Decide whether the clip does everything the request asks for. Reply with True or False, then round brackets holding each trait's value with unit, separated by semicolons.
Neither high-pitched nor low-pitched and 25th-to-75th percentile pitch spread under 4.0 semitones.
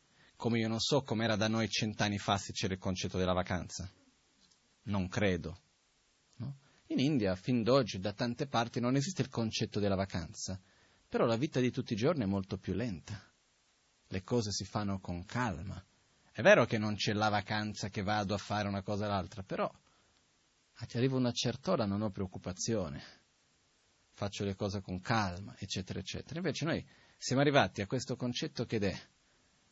False (105 Hz; 3.6 semitones)